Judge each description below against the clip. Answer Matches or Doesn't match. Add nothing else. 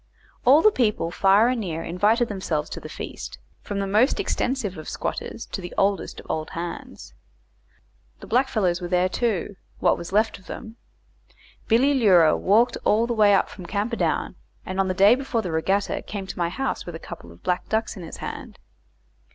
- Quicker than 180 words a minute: Matches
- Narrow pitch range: Doesn't match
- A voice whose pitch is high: Matches